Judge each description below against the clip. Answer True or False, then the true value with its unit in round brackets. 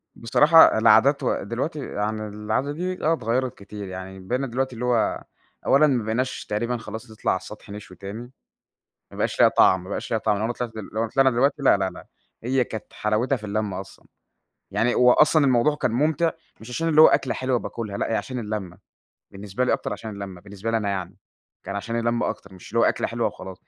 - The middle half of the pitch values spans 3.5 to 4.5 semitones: True (3.8 semitones)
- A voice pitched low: True (115 Hz)